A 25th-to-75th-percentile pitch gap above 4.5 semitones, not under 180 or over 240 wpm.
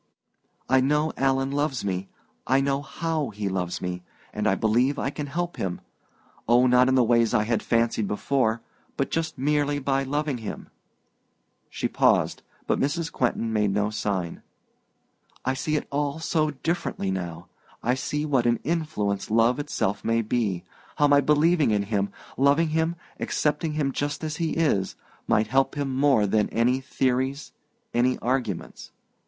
No: average, 4.9 semitones; average, 160 wpm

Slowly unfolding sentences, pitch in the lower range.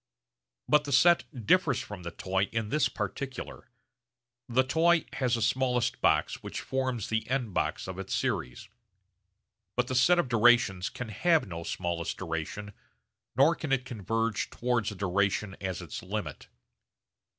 No: average, 150 wpm; low, 120 Hz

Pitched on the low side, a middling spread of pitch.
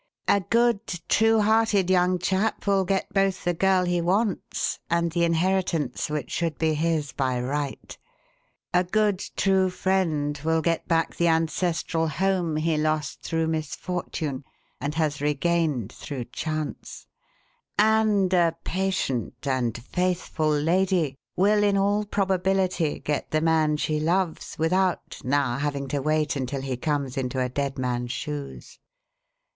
No: medium, 165 Hz; average, 4.3 semitones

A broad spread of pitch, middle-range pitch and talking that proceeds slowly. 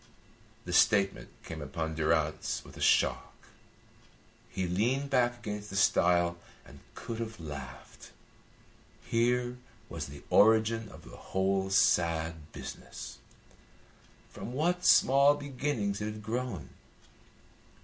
No: wide, 6.3 semitones; low, 105 Hz; slow, 115 wpm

